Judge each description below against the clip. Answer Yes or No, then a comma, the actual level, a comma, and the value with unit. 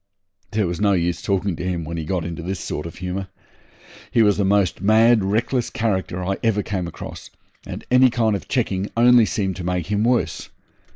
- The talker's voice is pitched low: Yes, very low, 95 Hz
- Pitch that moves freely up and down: No, average, 3.7 semitones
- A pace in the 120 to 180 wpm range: No, fast, 205 wpm